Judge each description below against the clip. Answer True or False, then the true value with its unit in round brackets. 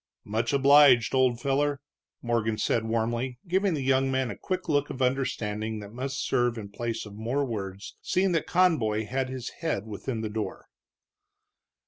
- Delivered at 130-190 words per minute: True (165 wpm)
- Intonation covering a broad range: False (3.8 semitones)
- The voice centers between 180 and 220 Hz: False (125 Hz)